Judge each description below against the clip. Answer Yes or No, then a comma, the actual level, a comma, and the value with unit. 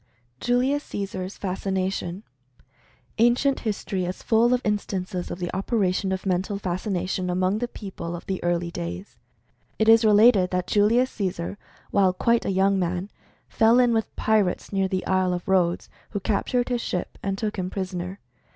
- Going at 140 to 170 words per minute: Yes, average, 160 wpm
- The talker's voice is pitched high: Yes, high, 195 Hz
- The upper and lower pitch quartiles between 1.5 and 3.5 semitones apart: Yes, average, 3.1 semitones